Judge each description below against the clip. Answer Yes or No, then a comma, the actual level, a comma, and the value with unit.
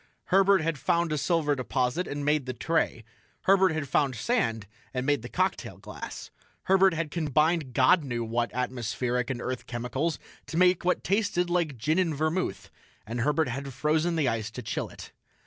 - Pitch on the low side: No, medium, 150 Hz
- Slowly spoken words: No, average, 180 wpm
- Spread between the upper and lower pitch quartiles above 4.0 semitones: Yes, average, 5.2 semitones